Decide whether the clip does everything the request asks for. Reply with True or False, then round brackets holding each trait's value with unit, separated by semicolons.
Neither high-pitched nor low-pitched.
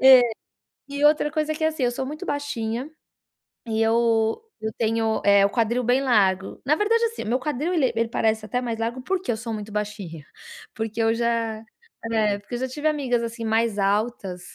False (230 Hz)